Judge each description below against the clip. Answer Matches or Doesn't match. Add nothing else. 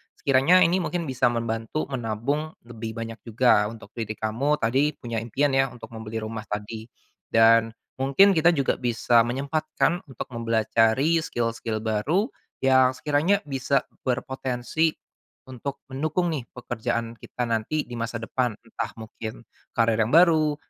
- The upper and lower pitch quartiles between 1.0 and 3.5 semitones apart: Doesn't match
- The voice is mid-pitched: Doesn't match